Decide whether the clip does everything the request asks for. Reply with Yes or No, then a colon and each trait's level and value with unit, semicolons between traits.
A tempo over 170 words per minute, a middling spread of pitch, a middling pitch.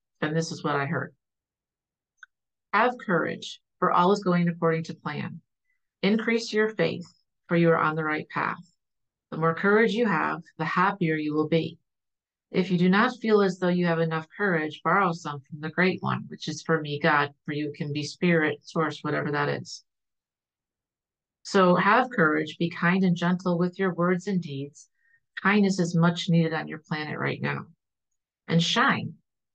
Yes: average, 180 wpm; average, 3.3 semitones; medium, 165 Hz